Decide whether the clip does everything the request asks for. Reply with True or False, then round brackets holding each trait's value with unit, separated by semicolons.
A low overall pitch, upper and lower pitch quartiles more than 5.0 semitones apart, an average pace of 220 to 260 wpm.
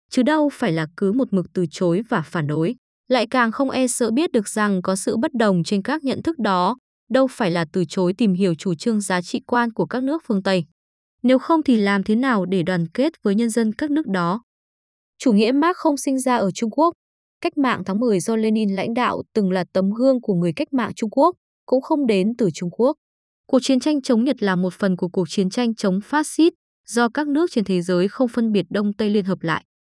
False (225 Hz; 5.5 semitones; 245 wpm)